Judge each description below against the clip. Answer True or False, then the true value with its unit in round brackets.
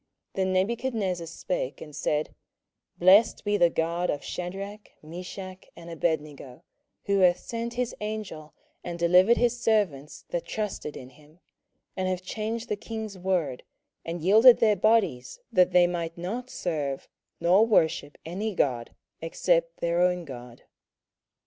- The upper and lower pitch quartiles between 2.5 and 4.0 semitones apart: False (4.4 semitones)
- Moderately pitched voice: True (180 Hz)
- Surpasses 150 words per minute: False (145 wpm)